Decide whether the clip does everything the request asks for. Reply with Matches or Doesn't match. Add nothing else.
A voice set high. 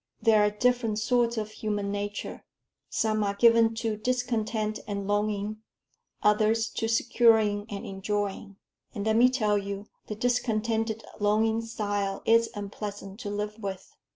Matches